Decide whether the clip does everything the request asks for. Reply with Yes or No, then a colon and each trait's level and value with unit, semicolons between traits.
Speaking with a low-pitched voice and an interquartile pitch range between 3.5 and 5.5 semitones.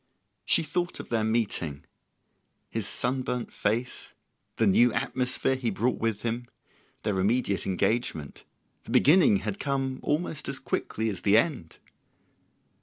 Yes: low, 120 Hz; average, 4.1 semitones